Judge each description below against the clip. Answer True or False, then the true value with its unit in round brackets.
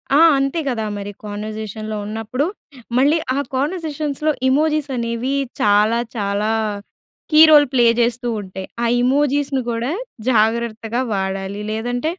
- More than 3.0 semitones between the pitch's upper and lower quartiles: True (4.6 semitones)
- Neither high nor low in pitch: False (235 Hz)